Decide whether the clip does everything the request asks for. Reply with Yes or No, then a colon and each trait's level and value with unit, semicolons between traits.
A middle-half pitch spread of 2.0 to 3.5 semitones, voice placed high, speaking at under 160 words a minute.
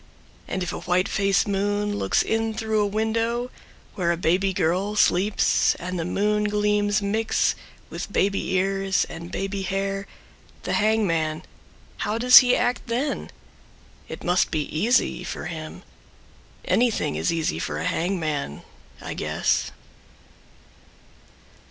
Yes: average, 3.2 semitones; high, 200 Hz; slow, 135 wpm